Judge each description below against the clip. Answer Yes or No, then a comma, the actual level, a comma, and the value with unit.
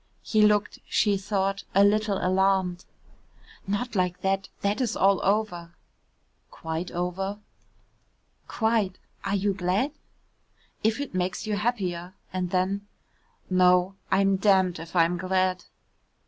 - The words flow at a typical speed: No, slow, 120 wpm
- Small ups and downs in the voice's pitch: Yes, narrow, 2.0 semitones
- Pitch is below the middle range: No, high, 190 Hz